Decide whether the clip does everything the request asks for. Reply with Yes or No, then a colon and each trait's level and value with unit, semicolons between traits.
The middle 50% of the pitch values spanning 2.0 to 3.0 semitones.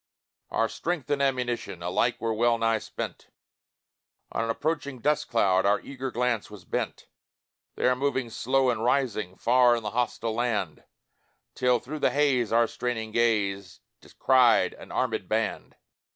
Yes: narrow, 2.6 semitones